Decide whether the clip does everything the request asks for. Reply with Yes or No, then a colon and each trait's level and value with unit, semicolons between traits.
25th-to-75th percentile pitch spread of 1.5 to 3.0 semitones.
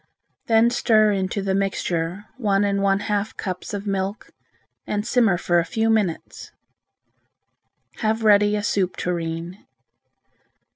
Yes: narrow, 2.5 semitones